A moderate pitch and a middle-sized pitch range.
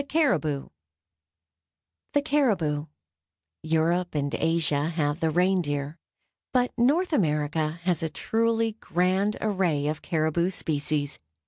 Yes: medium, 165 Hz; average, 4.2 semitones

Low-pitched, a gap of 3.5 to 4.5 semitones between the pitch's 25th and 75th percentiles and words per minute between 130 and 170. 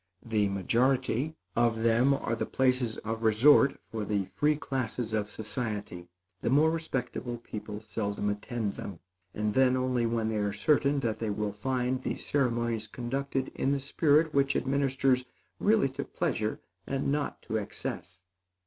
Yes: low, 120 Hz; average, 4.1 semitones; average, 155 wpm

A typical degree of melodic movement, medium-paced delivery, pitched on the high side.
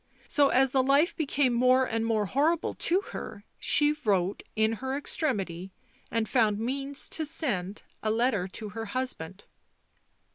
Yes: average, 4.9 semitones; average, 150 wpm; high, 245 Hz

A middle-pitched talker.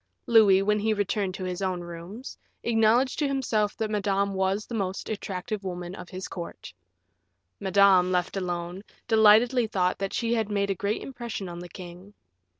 No: high, 200 Hz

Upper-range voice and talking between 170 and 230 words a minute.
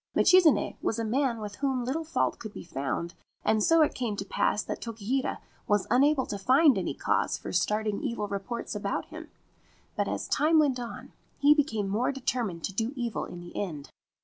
Yes: high, 235 Hz; average, 195 wpm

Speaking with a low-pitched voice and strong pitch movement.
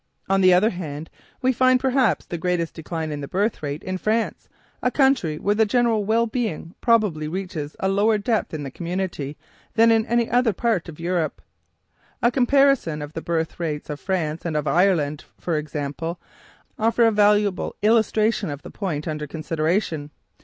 No: medium, 185 Hz; wide, 6.2 semitones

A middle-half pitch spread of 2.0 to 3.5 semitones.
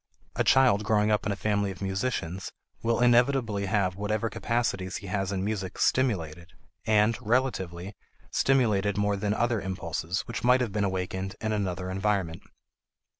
Yes: average, 3.0 semitones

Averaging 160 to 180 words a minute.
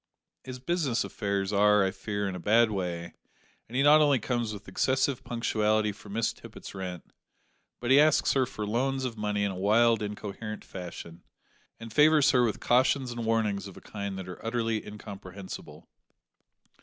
Yes: average, 175 wpm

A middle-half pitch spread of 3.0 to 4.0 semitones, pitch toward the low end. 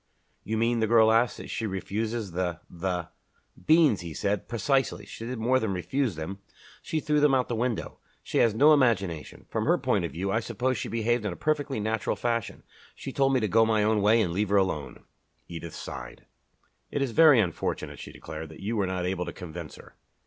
No: average, 4.7 semitones; low, 110 Hz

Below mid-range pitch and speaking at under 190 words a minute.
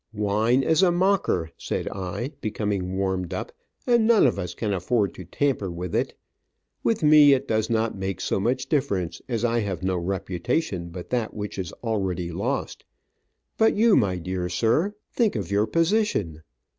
Yes: low, 105 Hz; average, 170 wpm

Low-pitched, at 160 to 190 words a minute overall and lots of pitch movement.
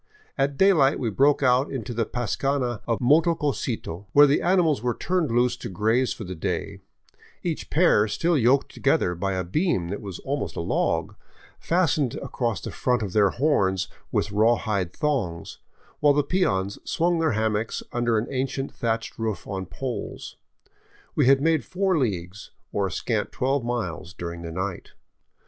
Yes: low, 120 Hz; average, 170 wpm; wide, 6.1 semitones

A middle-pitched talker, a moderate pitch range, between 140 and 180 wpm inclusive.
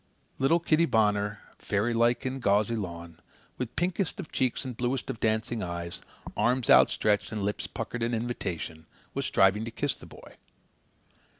No: low, 115 Hz; average, 3.7 semitones; average, 155 wpm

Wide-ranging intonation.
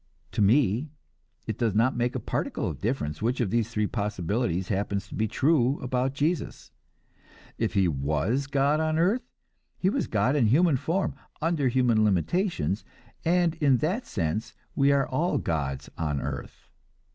Yes: wide, 6.7 semitones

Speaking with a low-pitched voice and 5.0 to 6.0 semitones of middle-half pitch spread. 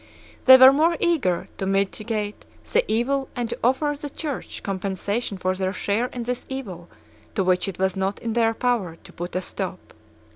No: high, 220 Hz; wide, 5.4 semitones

